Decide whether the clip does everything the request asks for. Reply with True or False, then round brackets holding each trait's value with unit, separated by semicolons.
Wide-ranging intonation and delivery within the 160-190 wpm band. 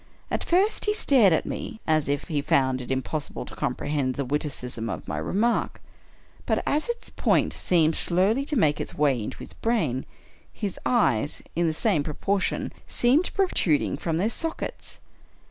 True (8.7 semitones; 170 wpm)